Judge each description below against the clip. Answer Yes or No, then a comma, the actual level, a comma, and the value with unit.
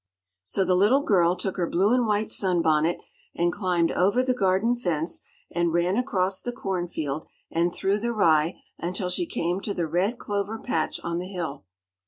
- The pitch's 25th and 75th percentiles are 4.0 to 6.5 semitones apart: No, average, 3.3 semitones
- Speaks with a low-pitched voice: No, medium, 185 Hz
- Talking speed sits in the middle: Yes, average, 190 wpm